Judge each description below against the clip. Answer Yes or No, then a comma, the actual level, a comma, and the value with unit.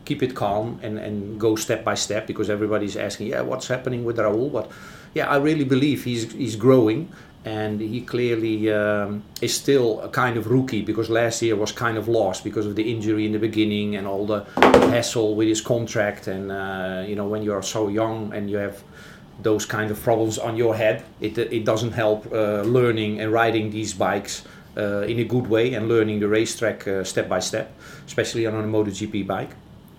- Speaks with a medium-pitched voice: No, low, 110 Hz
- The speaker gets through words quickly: Yes, fast, 210 wpm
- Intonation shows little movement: Yes, narrow, 1.8 semitones